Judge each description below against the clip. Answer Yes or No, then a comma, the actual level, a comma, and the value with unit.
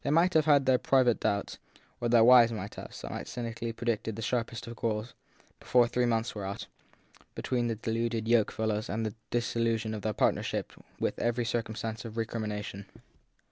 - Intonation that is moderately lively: No, narrow, 1.5 semitones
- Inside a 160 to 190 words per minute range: Yes, average, 185 wpm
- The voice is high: No, low, 115 Hz